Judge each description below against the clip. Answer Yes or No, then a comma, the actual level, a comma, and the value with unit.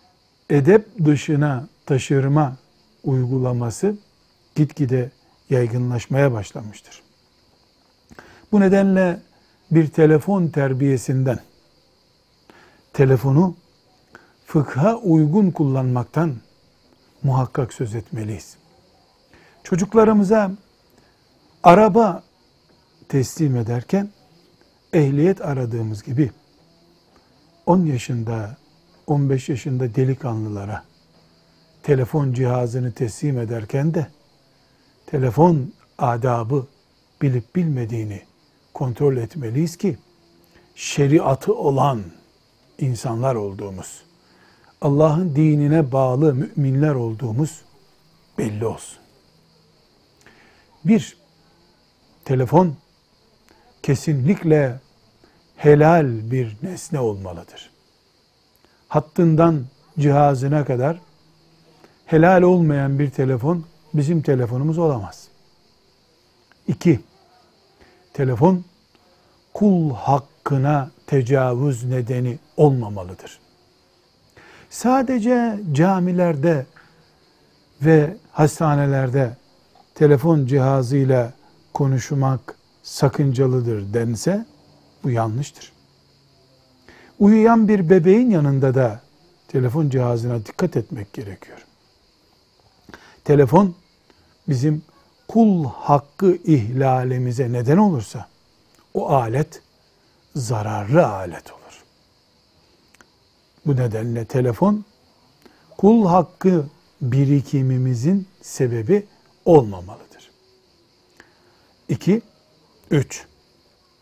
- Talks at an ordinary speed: No, slow, 65 wpm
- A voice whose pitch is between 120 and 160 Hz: Yes, medium, 140 Hz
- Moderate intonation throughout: Yes, average, 4.7 semitones